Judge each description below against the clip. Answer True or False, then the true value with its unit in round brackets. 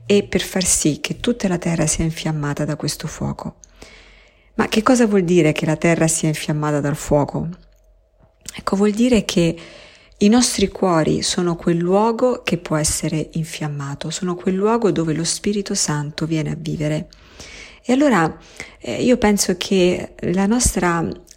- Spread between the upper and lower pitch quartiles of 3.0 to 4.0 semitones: False (4.5 semitones)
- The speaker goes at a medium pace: True (155 wpm)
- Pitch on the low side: False (175 Hz)